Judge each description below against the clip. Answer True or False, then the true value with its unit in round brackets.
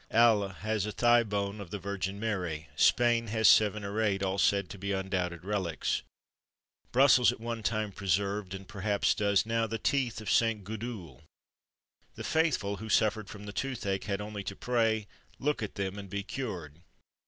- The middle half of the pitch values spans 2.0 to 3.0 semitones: True (2.4 semitones)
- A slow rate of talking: False (175 wpm)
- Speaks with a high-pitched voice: False (105 Hz)